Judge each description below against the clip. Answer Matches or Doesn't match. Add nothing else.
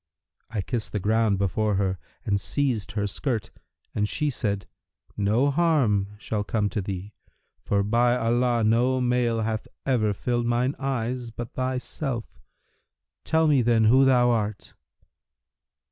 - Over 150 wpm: Doesn't match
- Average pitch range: Matches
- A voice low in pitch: Matches